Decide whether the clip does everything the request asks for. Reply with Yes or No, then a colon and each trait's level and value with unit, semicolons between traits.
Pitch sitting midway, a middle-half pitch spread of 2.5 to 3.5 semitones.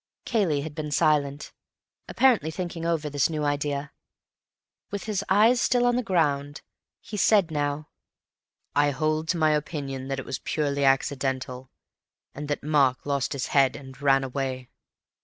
Yes: medium, 145 Hz; average, 2.8 semitones